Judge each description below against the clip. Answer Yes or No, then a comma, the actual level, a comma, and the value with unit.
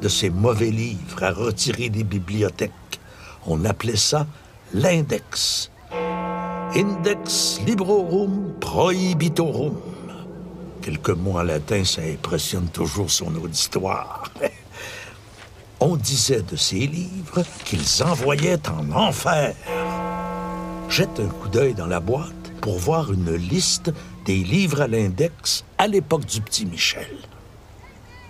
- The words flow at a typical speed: No, slow, 110 wpm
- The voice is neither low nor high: No, low, 130 Hz